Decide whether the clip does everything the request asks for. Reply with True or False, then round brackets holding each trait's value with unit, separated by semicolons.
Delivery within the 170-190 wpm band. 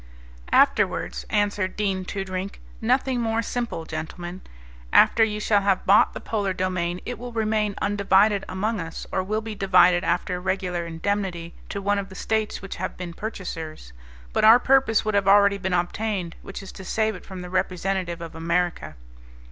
True (175 wpm)